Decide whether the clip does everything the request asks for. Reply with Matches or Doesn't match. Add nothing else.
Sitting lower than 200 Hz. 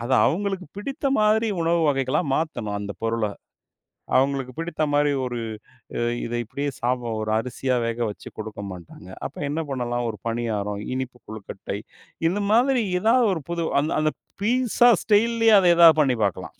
Matches